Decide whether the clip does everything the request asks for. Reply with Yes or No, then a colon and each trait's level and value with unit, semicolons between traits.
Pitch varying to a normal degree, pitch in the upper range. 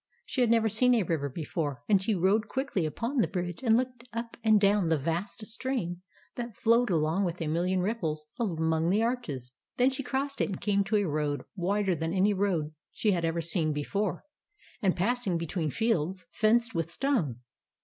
No: wide, 5.7 semitones; high, 195 Hz